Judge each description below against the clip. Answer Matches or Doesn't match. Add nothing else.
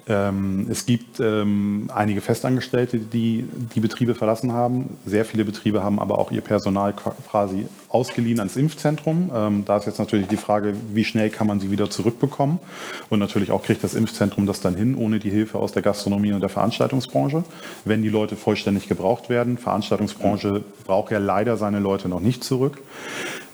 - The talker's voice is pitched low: Matches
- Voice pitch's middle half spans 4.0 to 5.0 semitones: Doesn't match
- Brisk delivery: Doesn't match